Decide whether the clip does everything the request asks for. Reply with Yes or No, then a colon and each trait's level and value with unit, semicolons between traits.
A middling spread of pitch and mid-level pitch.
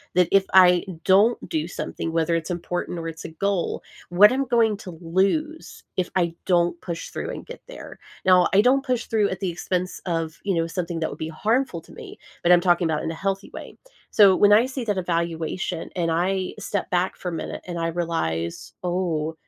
Yes: average, 3.0 semitones; medium, 180 Hz